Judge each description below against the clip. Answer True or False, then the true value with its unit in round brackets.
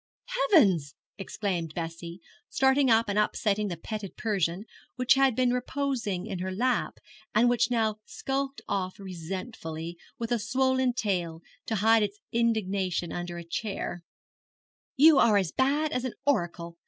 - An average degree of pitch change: False (5.8 semitones)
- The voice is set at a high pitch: True (210 Hz)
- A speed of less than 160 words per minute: True (145 wpm)